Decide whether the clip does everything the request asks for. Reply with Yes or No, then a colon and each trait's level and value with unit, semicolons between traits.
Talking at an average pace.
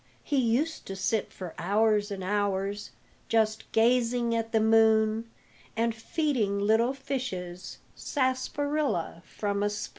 No: slow, 125 wpm